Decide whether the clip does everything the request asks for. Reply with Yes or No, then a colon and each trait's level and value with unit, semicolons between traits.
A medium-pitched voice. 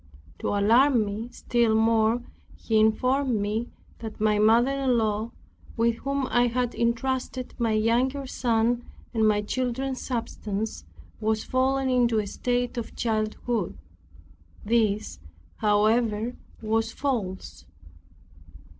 No: high, 230 Hz